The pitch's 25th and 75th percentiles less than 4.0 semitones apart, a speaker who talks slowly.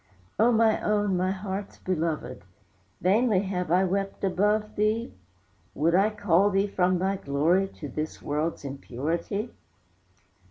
Yes: average, 3.6 semitones; slow, 130 wpm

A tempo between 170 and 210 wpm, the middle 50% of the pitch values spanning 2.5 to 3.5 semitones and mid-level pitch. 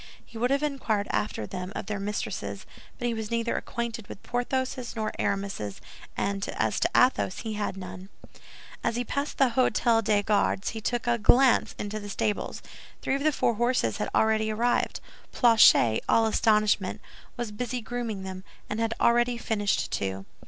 No: average, 175 wpm; average, 2.9 semitones; high, 220 Hz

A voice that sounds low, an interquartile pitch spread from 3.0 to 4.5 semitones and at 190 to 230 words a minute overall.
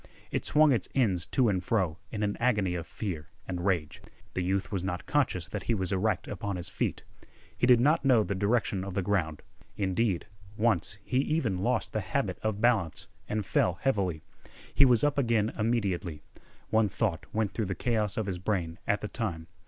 Yes: low, 100 Hz; average, 4.0 semitones; average, 195 wpm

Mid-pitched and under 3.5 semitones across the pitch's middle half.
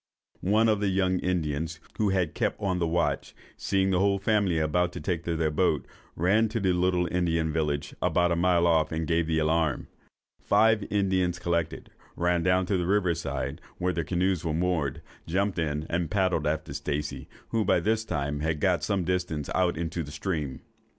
No: very low, 85 Hz; average, 2.8 semitones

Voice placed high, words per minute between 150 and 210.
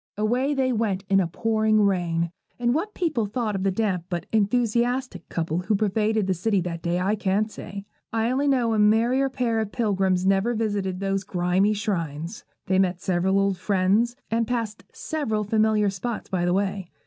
Yes: high, 205 Hz; average, 185 wpm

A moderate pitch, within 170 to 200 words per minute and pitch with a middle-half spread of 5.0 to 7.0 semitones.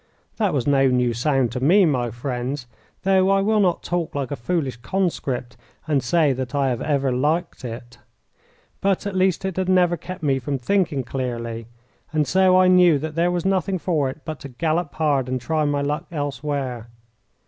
Yes: medium, 145 Hz; average, 190 wpm; wide, 5.5 semitones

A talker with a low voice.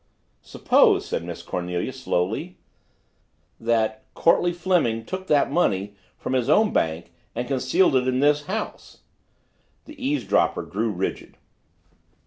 Yes: low, 130 Hz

